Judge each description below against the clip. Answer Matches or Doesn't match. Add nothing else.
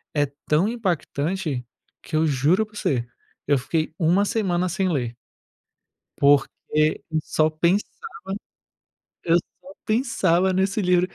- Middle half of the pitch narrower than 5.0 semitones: Matches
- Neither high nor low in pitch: Matches